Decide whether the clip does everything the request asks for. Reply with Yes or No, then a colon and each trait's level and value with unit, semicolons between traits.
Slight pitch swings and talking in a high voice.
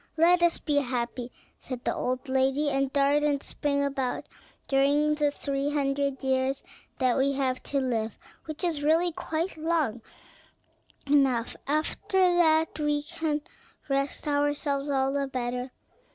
Yes: narrow, 2.2 semitones; very high, 280 Hz